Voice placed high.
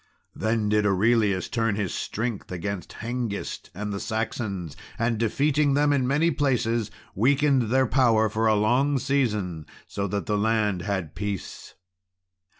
No: low, 110 Hz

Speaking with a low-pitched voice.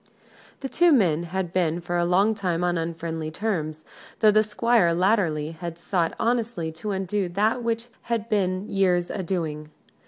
No: medium, 180 Hz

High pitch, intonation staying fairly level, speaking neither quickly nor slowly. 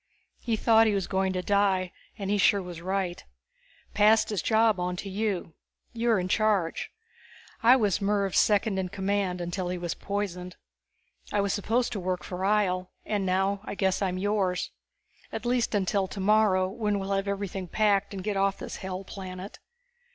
Yes: high, 195 Hz; narrow, 2.0 semitones; average, 175 wpm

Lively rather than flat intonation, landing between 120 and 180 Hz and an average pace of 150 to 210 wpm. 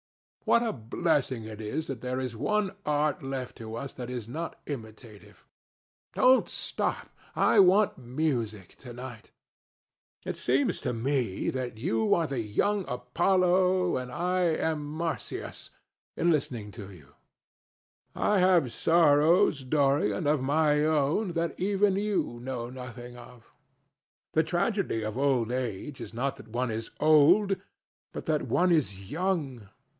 No: wide, 6.0 semitones; low, 135 Hz; average, 140 wpm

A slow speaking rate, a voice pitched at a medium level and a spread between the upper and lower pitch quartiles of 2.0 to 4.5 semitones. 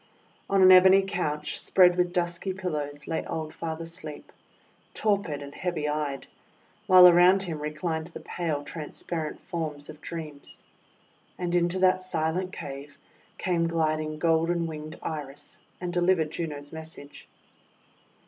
Yes: slow, 130 wpm; medium, 165 Hz; average, 2.8 semitones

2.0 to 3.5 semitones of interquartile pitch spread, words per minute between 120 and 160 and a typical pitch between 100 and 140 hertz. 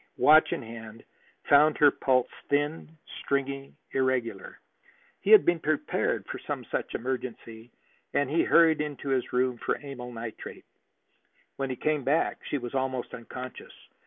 Yes: average, 3.1 semitones; average, 145 wpm; low, 135 Hz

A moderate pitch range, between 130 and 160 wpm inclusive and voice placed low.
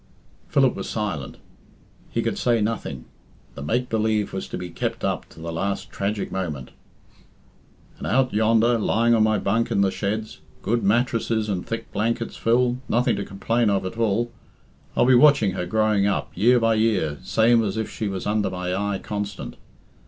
No: average, 3.0 semitones; average, 180 wpm; low, 110 Hz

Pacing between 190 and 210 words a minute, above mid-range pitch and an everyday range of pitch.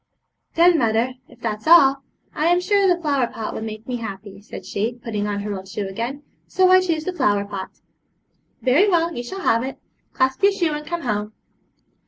No: average, 200 wpm; very high, 255 Hz; wide, 8.1 semitones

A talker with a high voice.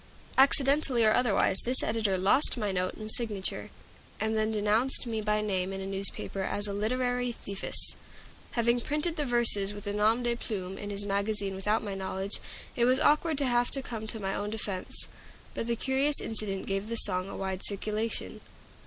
Yes: high, 215 Hz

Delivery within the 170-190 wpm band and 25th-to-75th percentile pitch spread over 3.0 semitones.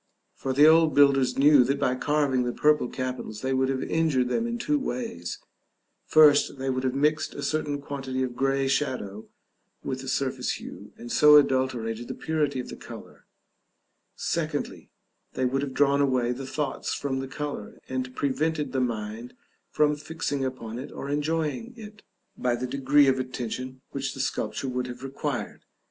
No: average, 175 wpm; narrow, 2.4 semitones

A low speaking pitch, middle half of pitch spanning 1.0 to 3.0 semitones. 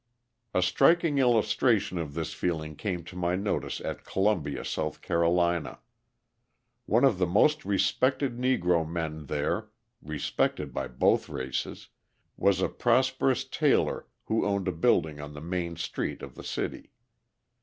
No: very low, 90 Hz; average, 4.6 semitones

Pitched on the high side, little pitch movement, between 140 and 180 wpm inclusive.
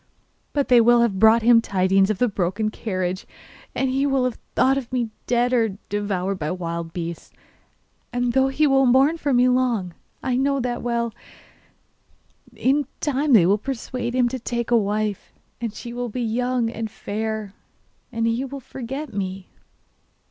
No: high, 235 Hz; average, 3.8 semitones; average, 170 wpm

